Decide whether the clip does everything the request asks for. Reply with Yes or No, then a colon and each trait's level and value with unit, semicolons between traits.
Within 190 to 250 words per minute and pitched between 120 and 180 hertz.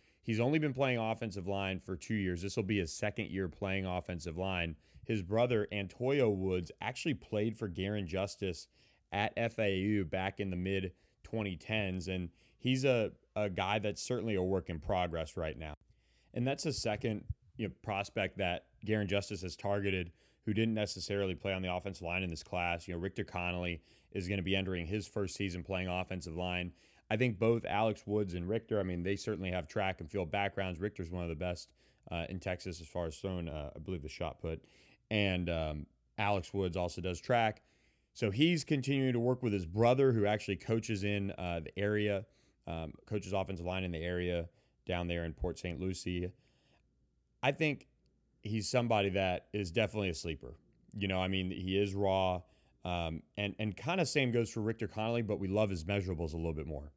No: average, 200 wpm; very low, 95 Hz